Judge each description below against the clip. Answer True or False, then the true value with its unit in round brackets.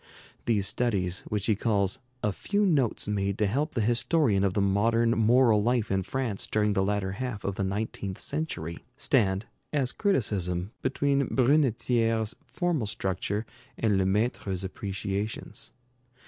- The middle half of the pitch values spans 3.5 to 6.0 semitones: True (4.1 semitones)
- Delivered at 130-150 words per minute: True (140 wpm)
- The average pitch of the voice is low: True (105 Hz)